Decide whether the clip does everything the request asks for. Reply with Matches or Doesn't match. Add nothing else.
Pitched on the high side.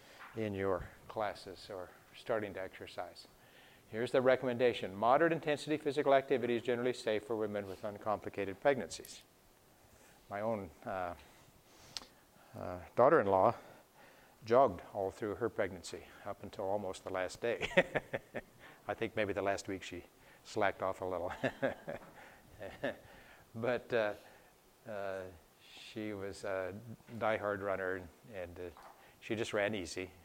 Doesn't match